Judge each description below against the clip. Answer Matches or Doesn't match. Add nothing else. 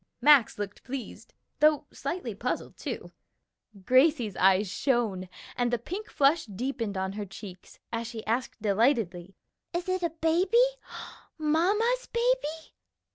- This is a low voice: Doesn't match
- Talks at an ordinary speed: Doesn't match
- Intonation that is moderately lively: Doesn't match